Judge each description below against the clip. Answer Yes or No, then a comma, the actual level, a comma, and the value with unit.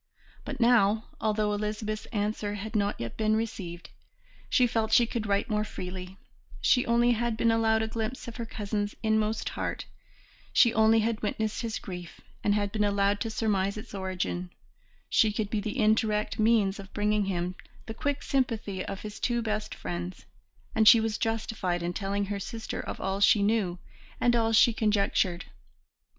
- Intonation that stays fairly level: Yes, narrow, 2.0 semitones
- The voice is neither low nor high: No, high, 215 Hz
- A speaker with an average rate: Yes, average, 175 wpm